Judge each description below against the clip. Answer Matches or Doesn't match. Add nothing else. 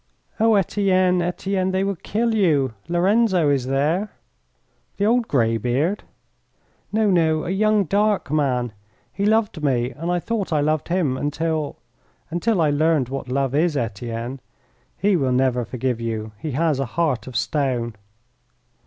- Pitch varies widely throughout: Matches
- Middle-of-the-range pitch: Matches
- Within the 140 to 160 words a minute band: Matches